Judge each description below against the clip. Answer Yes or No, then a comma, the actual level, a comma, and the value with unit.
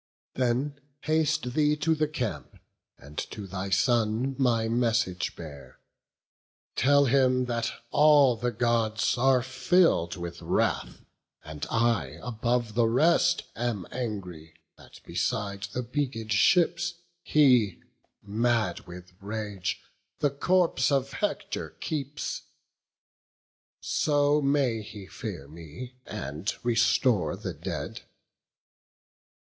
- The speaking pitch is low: Yes, low, 120 Hz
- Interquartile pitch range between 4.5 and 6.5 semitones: Yes, wide, 5.4 semitones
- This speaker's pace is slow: Yes, slow, 110 wpm